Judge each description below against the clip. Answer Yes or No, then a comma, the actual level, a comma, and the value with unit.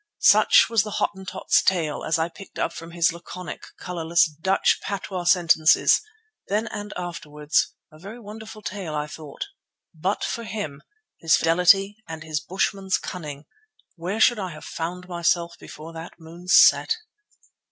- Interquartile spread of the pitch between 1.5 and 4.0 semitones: Yes, average, 3.3 semitones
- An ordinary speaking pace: Yes, average, 150 wpm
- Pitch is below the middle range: No, medium, 175 Hz